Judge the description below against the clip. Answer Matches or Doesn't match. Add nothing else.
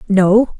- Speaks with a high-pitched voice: Matches